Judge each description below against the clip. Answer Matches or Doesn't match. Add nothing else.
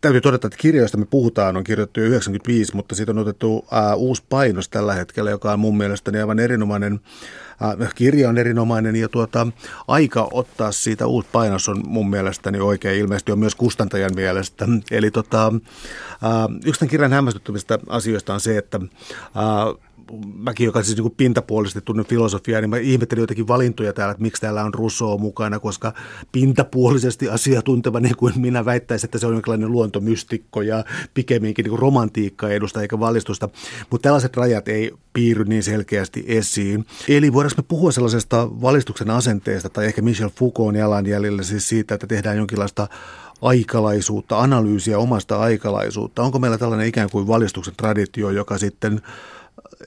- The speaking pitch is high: Doesn't match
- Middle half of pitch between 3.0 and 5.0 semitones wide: Doesn't match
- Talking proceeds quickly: Matches